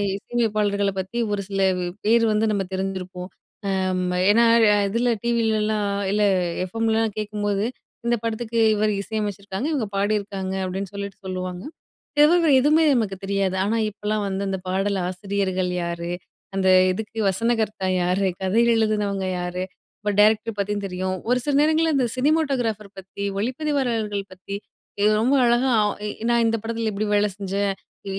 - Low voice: No, high, 205 Hz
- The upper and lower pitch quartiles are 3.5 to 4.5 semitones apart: No, average, 2.8 semitones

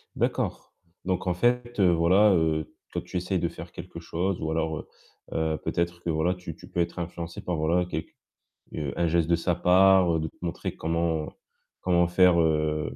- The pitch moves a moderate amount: No, narrow, 1.9 semitones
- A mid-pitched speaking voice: No, very low, 85 Hz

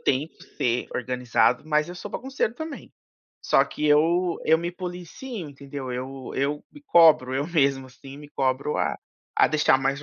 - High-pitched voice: No, medium, 145 Hz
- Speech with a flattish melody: No, average, 4.5 semitones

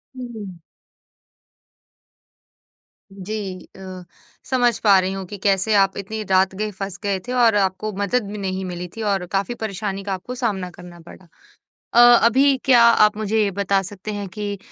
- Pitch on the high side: Yes, high, 200 Hz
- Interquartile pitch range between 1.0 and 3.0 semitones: Yes, narrow, 2.5 semitones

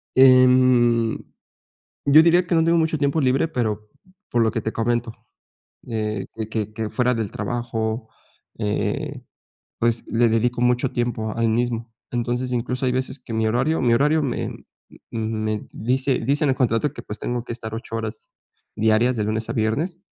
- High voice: No, low, 120 Hz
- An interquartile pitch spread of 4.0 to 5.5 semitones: No, narrow, 2.5 semitones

